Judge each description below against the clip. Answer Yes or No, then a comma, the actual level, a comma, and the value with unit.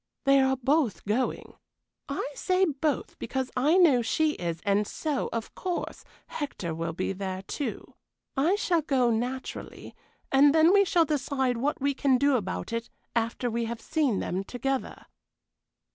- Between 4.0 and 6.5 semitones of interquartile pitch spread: Yes, average, 4.4 semitones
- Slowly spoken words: No, average, 160 wpm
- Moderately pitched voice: No, very high, 265 Hz